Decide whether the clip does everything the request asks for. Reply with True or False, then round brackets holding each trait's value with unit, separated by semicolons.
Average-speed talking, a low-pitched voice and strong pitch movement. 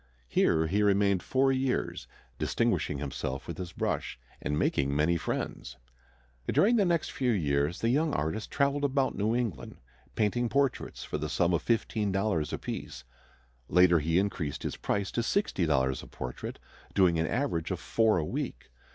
True (160 wpm; 95 Hz; 7.5 semitones)